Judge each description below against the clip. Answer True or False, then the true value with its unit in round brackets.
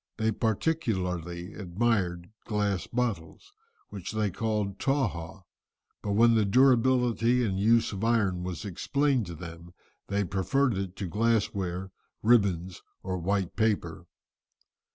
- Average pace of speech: False (125 wpm)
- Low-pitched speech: True (100 Hz)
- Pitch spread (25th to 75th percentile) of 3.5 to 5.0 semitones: True (4.1 semitones)